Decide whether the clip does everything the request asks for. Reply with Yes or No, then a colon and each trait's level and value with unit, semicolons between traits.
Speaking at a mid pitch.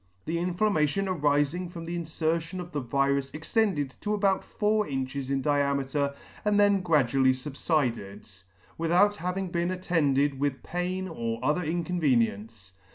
Yes: medium, 155 Hz